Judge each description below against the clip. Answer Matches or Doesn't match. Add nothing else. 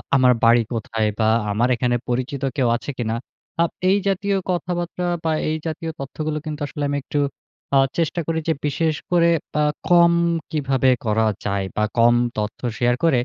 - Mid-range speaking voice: Matches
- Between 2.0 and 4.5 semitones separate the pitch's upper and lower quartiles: Doesn't match